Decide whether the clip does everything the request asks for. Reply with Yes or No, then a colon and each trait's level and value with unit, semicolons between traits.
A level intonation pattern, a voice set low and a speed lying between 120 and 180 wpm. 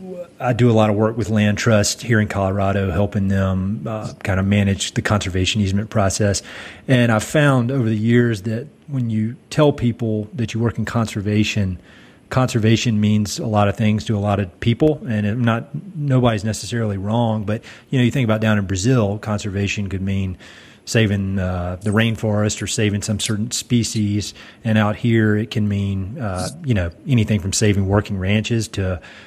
No: narrow, 2.3 semitones; low, 110 Hz; average, 190 wpm